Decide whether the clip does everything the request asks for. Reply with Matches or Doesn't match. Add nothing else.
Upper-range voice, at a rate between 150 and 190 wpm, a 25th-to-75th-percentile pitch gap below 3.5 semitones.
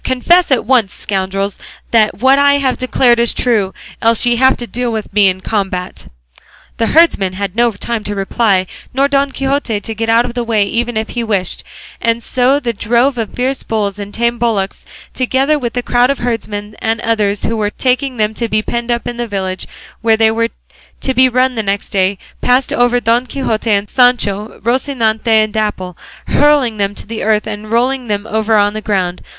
Doesn't match